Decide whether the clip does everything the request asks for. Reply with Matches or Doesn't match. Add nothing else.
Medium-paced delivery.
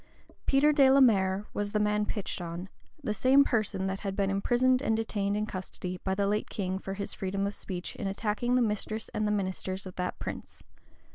Doesn't match